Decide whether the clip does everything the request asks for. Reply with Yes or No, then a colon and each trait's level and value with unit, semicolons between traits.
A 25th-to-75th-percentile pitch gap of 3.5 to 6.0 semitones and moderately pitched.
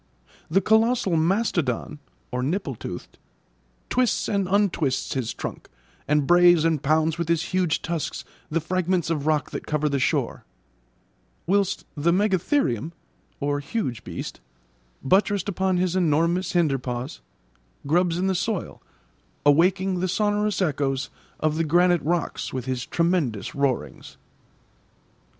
Yes: average, 4.3 semitones; medium, 170 Hz